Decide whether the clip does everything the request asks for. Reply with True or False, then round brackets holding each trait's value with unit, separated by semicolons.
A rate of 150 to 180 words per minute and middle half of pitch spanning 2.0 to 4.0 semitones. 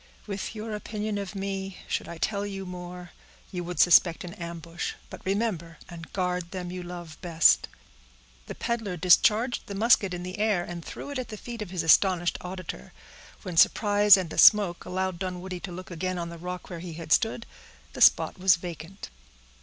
False (190 wpm; 2.6 semitones)